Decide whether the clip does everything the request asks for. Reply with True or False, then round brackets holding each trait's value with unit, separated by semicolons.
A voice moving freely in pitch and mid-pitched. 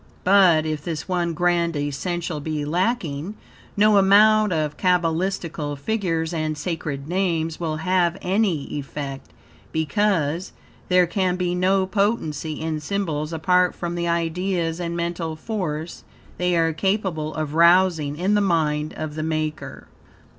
False (3.0 semitones; 170 Hz)